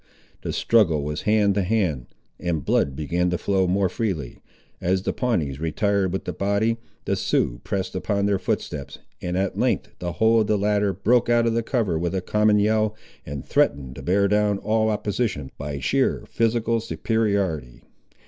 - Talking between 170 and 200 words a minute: Yes, average, 175 wpm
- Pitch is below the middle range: Yes, low, 100 Hz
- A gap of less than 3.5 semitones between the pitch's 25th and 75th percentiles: No, average, 4.8 semitones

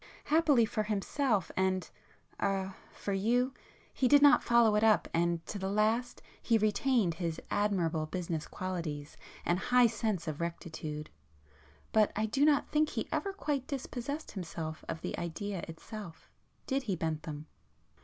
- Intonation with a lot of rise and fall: Yes, wide, 6.3 semitones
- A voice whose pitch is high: Yes, high, 205 Hz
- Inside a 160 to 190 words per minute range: No, average, 145 wpm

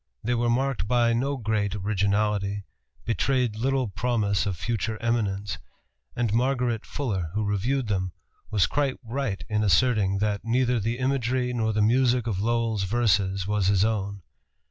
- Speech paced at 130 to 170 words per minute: Yes, average, 150 wpm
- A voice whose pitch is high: No, low, 110 Hz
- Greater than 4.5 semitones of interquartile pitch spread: No, average, 3.3 semitones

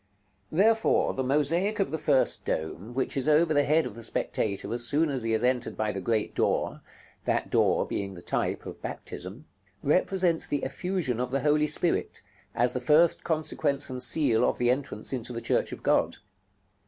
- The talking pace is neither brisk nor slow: Yes, average, 195 wpm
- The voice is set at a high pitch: No, low, 135 Hz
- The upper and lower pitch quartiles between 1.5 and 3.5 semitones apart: No, average, 4.9 semitones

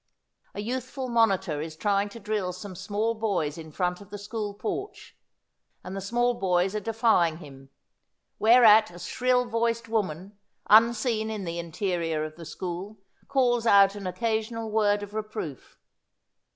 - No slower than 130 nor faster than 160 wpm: Yes, average, 155 wpm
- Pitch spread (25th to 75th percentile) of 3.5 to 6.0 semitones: Yes, average, 4.0 semitones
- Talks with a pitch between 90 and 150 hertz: No, high, 205 Hz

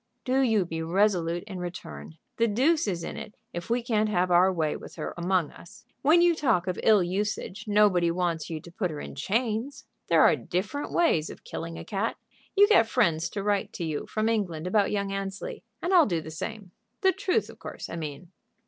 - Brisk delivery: Yes, fast, 210 wpm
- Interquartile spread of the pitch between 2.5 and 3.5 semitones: No, average, 4.6 semitones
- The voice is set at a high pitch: Yes, high, 195 Hz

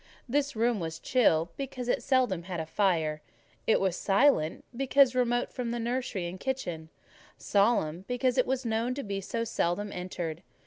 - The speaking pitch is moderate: No, high, 225 Hz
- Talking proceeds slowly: No, average, 170 wpm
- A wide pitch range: Yes, wide, 6.3 semitones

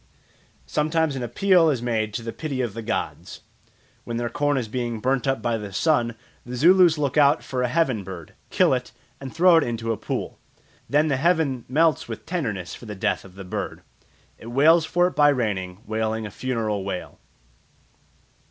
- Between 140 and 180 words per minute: No, average, 190 wpm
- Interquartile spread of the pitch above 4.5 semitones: Yes, average, 5.3 semitones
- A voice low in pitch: Yes, low, 125 Hz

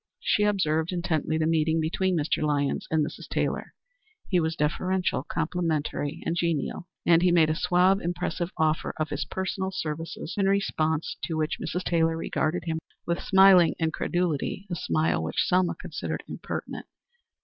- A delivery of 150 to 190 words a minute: Yes, average, 155 wpm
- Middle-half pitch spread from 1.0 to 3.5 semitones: Yes, narrow, 2.5 semitones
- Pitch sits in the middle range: Yes, medium, 165 Hz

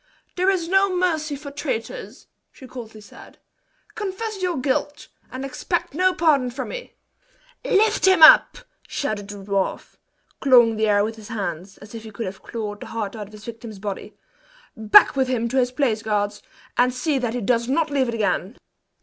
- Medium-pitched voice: No, high, 245 Hz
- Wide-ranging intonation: Yes, wide, 5.8 semitones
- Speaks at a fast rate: No, average, 185 wpm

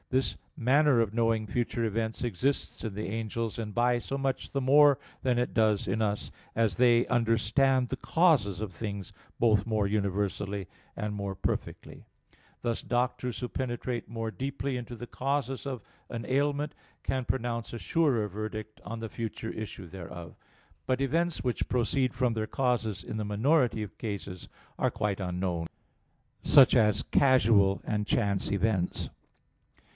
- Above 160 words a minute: No, average, 155 wpm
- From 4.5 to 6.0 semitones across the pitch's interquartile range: No, average, 3.6 semitones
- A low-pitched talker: Yes, low, 115 Hz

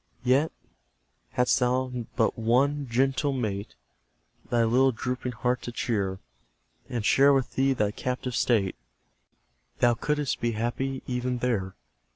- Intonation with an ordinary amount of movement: No, narrow, 2.3 semitones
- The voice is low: Yes, low, 125 Hz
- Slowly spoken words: Yes, slow, 130 wpm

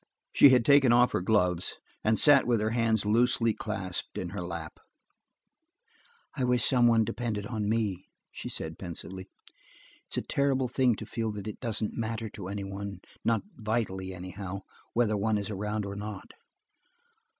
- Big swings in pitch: No, average, 3.1 semitones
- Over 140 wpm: Yes, average, 150 wpm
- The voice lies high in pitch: No, low, 110 Hz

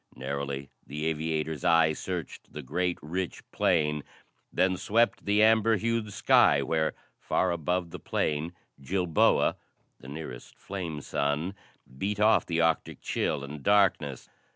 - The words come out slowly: Yes, slow, 130 wpm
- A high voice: No, very low, 80 Hz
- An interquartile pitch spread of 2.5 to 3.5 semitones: No, average, 4.1 semitones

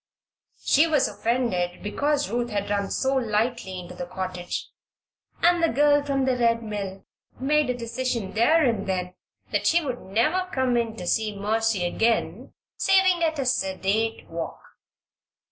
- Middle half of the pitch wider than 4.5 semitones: Yes, wide, 5.4 semitones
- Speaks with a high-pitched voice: Yes, high, 230 Hz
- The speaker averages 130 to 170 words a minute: Yes, average, 155 wpm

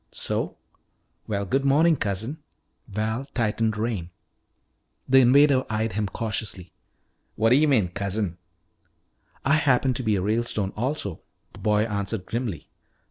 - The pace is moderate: No, slow, 130 wpm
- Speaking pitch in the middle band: No, low, 110 Hz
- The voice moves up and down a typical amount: Yes, average, 4.2 semitones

